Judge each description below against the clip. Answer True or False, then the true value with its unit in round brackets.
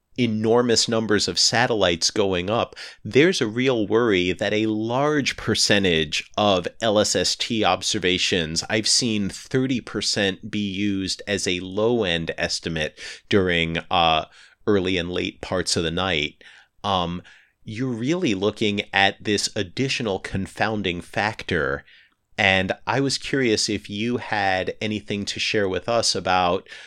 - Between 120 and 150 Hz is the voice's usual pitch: False (105 Hz)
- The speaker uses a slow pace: True (130 wpm)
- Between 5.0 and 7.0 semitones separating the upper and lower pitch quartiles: False (3.3 semitones)